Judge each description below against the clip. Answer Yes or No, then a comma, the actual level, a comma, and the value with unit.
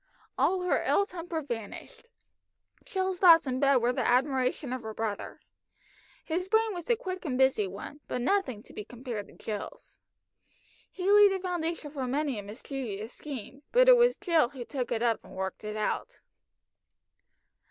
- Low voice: No, very high, 275 Hz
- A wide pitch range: Yes, wide, 7.5 semitones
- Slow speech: No, average, 175 wpm